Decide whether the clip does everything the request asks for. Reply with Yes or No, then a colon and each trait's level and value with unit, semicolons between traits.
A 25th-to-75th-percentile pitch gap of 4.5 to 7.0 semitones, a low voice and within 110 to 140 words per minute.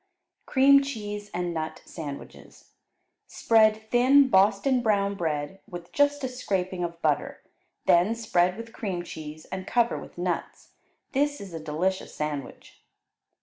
No: average, 5.2 semitones; high, 195 Hz; slow, 135 wpm